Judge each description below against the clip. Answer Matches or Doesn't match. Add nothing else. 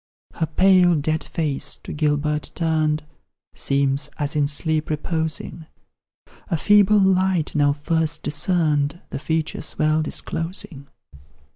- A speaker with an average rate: Doesn't match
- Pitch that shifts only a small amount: Matches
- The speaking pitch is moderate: Matches